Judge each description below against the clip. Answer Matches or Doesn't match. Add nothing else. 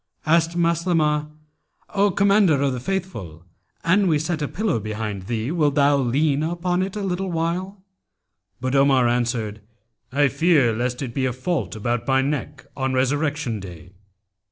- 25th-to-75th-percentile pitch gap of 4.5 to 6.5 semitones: Matches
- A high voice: Doesn't match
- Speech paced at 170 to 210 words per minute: Doesn't match